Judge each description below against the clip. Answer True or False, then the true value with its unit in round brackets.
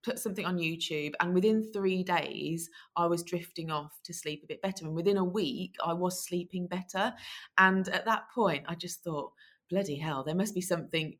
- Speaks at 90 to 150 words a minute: False (205 wpm)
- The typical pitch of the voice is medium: True (180 Hz)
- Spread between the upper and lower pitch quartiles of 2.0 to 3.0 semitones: True (2.6 semitones)